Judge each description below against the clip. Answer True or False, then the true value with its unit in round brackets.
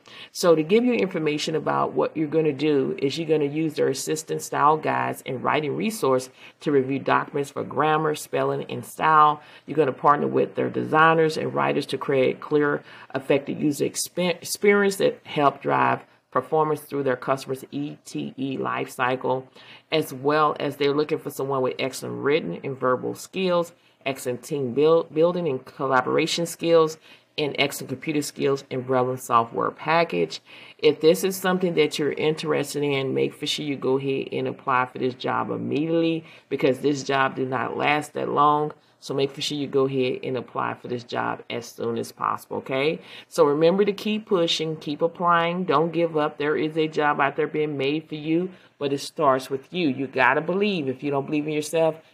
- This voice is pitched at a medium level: True (150 Hz)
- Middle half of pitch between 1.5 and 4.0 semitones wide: True (3.1 semitones)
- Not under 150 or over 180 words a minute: False (190 wpm)